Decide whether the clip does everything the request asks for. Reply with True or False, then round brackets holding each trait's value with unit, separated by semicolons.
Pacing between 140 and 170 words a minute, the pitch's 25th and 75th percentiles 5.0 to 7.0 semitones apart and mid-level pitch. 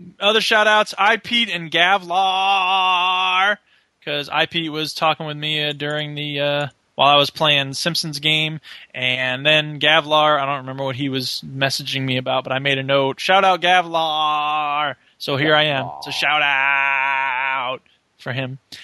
False (155 wpm; 4.0 semitones; 150 Hz)